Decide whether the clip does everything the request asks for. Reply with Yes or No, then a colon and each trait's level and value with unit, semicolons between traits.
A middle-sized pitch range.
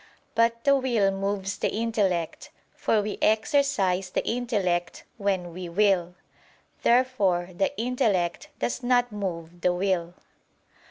Yes: average, 4.5 semitones